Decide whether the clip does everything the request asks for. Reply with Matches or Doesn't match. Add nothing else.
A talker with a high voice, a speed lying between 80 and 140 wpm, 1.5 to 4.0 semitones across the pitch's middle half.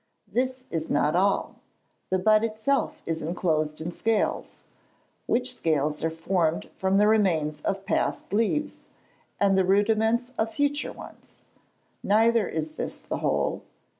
Doesn't match